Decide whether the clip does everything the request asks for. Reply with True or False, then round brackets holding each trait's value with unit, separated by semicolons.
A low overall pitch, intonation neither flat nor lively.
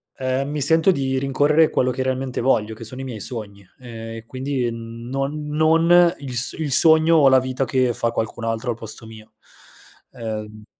True (130 Hz; 4.0 semitones)